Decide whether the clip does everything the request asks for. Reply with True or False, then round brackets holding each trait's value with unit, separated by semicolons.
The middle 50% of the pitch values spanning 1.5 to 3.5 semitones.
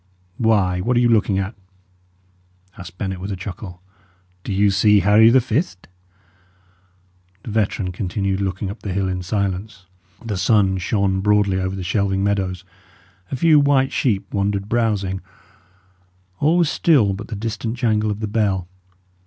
True (2.7 semitones)